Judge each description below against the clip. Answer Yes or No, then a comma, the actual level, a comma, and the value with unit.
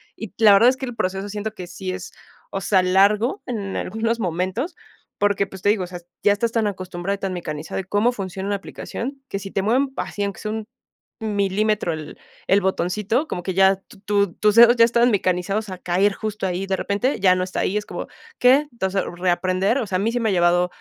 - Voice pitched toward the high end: Yes, high, 200 Hz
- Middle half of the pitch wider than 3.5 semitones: No, average, 3.0 semitones